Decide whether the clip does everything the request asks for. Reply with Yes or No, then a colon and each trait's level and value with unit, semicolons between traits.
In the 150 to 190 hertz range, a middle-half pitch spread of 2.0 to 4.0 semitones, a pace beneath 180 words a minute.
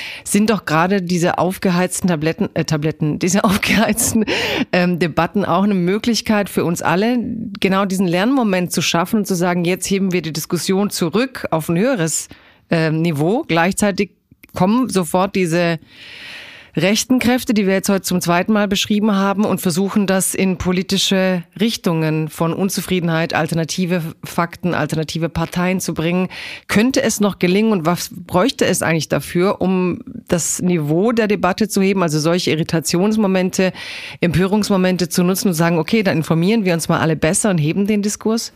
Yes: medium, 185 Hz; average, 3.2 semitones; average, 160 wpm